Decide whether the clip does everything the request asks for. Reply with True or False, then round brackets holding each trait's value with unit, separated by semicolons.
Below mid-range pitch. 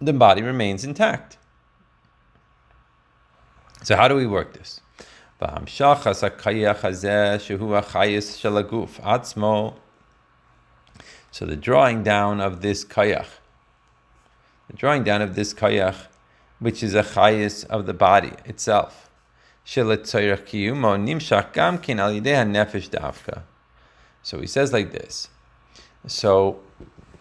True (105 Hz)